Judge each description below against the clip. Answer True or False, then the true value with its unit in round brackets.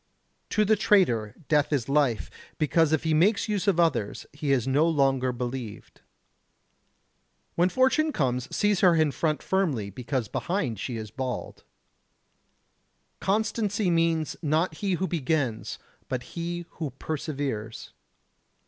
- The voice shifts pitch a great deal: True (5.7 semitones)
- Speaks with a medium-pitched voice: True (155 Hz)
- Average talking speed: False (130 wpm)